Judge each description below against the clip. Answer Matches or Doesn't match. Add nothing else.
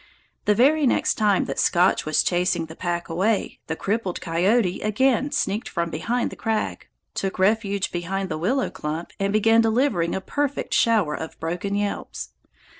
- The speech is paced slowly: Doesn't match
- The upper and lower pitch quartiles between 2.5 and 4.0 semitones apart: Doesn't match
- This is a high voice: Matches